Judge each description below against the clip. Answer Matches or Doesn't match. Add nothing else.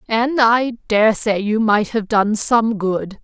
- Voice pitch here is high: Matches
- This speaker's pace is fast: Doesn't match